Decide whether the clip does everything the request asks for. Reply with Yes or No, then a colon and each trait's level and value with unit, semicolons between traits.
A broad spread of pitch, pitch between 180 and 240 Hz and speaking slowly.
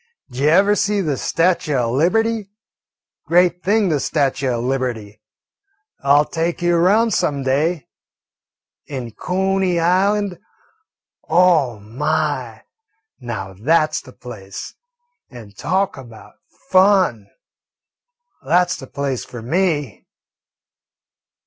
No: wide, 6.5 semitones; medium, 155 Hz; slow, 110 wpm